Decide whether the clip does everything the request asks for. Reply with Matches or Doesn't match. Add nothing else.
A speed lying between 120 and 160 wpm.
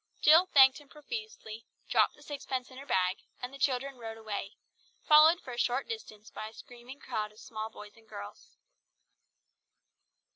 Doesn't match